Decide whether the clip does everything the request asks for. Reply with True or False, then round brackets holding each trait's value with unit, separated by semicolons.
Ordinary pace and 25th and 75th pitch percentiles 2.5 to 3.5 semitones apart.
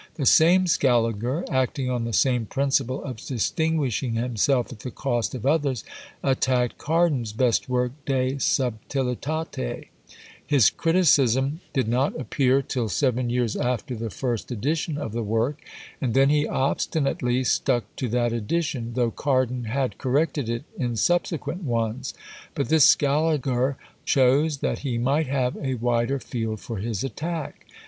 True (145 wpm; 3.0 semitones)